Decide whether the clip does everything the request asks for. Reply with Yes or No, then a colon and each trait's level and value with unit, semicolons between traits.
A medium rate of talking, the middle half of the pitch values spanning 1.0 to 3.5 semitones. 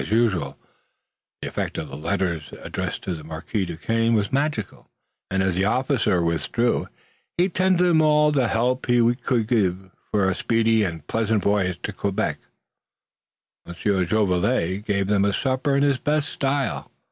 No: average, 160 wpm; wide, 5.6 semitones